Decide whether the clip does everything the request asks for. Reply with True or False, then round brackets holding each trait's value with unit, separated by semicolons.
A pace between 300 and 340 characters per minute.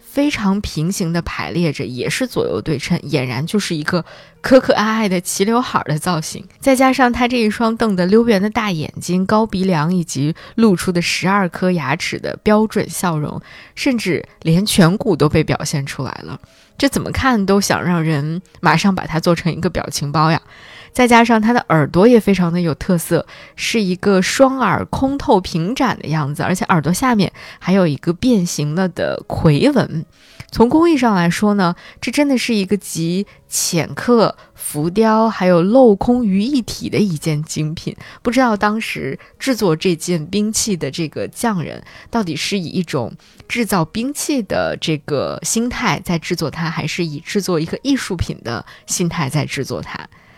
False (260 characters per minute)